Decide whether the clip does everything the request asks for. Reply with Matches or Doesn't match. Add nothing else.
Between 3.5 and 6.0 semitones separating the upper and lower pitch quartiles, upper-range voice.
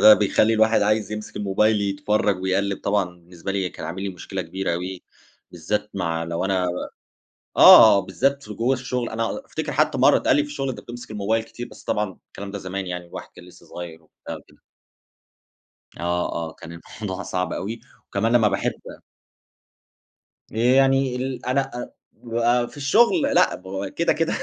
Doesn't match